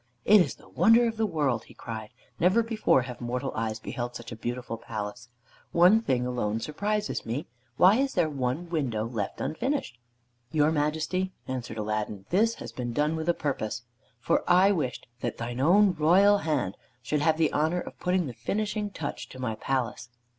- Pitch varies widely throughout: Yes, wide, 7.4 semitones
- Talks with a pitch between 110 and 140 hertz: No, medium, 150 Hz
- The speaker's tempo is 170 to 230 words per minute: Yes, average, 185 wpm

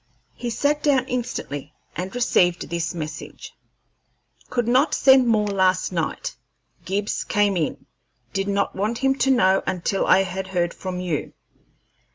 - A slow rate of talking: No, average, 145 wpm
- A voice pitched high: Yes, high, 195 Hz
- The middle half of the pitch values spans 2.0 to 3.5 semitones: No, average, 5.0 semitones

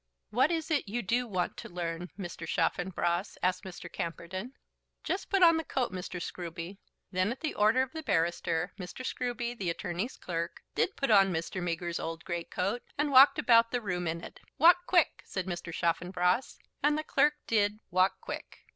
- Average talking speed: Yes, average, 185 wpm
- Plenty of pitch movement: Yes, wide, 6.4 semitones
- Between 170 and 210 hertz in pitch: Yes, high, 190 Hz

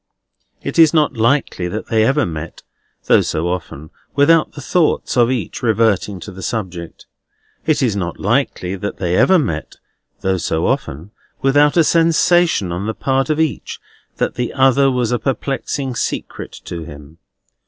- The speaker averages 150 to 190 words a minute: Yes, average, 165 wpm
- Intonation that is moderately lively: No, wide, 7.7 semitones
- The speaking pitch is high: No, low, 115 Hz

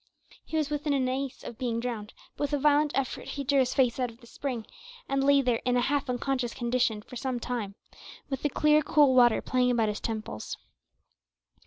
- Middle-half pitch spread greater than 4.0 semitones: No, average, 2.8 semitones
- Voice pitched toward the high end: Yes, very high, 255 Hz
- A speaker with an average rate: No, fast, 210 wpm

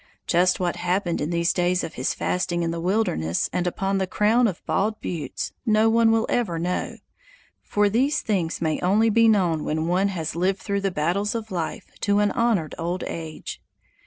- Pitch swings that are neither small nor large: Yes, average, 3.8 semitones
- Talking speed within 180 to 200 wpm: Yes, average, 190 wpm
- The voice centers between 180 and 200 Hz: Yes, medium, 185 Hz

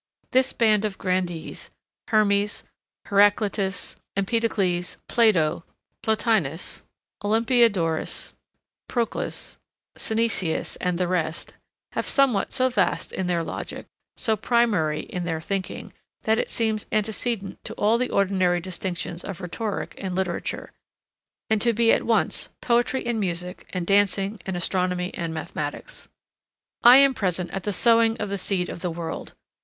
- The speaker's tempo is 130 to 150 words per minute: Yes, slow, 135 wpm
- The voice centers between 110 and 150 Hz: No, high, 200 Hz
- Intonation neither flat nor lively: Yes, average, 3.9 semitones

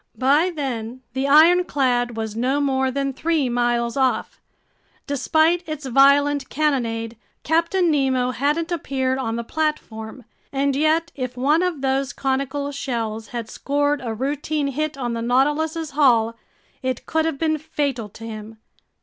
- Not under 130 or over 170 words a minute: Yes, average, 145 wpm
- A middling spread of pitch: Yes, average, 3.6 semitones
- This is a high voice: Yes, very high, 275 Hz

